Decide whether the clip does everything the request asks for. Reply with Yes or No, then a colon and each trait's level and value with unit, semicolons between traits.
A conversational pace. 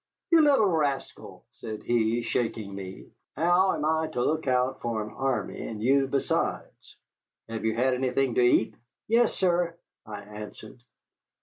Yes: average, 150 wpm